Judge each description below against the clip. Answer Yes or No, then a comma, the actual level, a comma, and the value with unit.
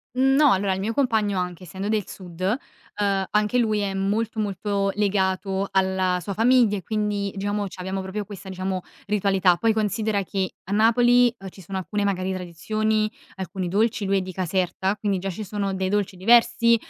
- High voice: Yes, high, 200 Hz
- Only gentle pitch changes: Yes, narrow, 2.1 semitones